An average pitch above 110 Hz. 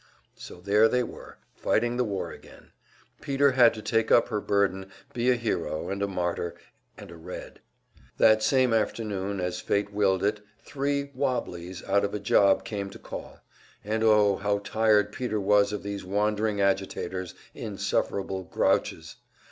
No: low, 105 Hz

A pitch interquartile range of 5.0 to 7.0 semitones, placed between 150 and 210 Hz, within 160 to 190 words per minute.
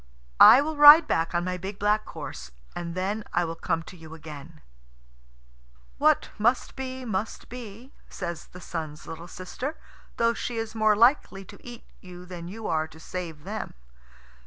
Yes: average, 5.3 semitones; medium, 185 Hz; average, 165 wpm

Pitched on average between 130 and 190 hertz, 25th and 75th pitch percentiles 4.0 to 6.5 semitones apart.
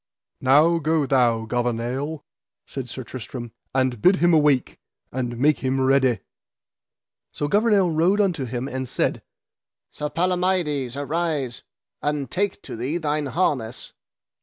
Yes: medium, 140 Hz; average, 4.4 semitones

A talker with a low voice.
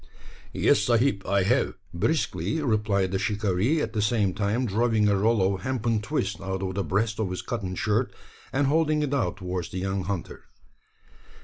Yes: low, 105 Hz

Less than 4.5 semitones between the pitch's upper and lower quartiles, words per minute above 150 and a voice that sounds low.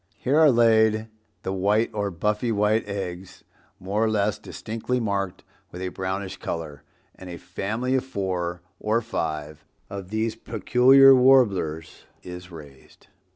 No: average, 4.0 semitones; average, 140 wpm; low, 100 Hz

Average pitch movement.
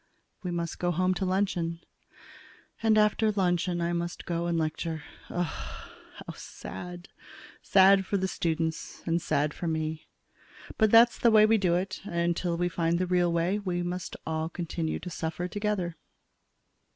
No: narrow, 2.1 semitones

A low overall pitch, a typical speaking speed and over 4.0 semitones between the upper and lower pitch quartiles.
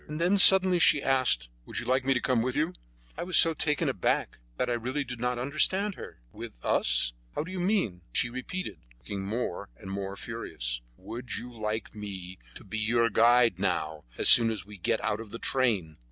No: low, 115 Hz; fast, 210 wpm; wide, 5.4 semitones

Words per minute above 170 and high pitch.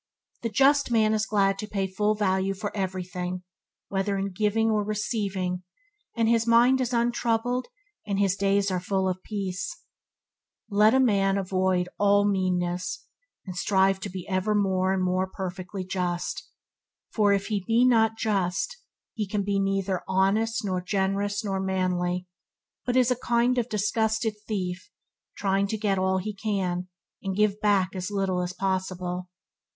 No: average, 155 wpm; high, 195 Hz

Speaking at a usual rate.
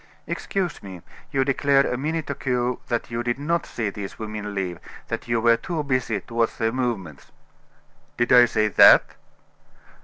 Yes: average, 165 wpm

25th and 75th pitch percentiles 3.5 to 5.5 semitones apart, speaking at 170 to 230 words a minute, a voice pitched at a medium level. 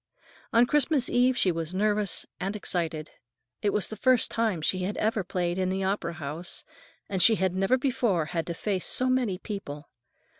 No: average, 4.6 semitones; average, 185 wpm; high, 195 Hz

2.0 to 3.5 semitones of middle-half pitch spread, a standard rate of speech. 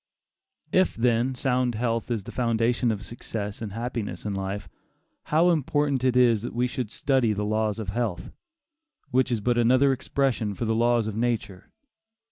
Yes: average, 2.7 semitones; average, 170 wpm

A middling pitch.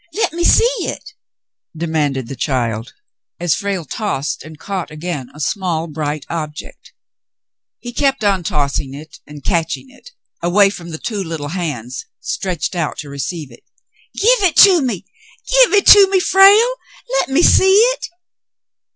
Yes: medium, 170 Hz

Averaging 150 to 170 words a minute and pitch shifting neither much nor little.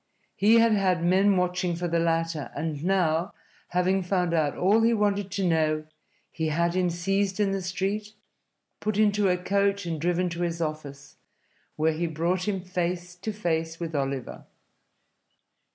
Yes: average, 165 wpm; average, 3.0 semitones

